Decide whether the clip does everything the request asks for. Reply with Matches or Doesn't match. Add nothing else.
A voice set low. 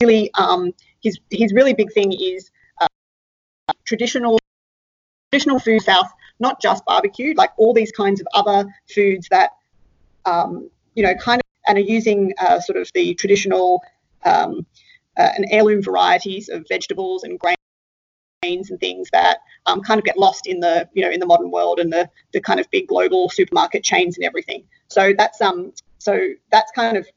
Doesn't match